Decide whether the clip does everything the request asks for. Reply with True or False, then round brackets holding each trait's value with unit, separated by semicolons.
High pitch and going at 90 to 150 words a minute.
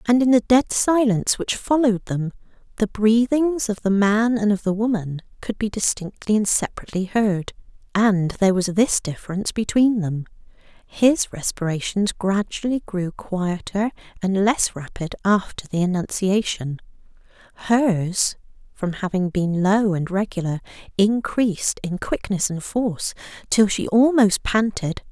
True (205 Hz; 135 wpm)